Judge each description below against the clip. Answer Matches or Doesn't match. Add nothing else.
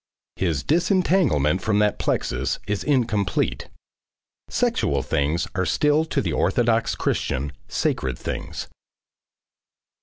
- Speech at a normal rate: Doesn't match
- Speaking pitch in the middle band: Doesn't match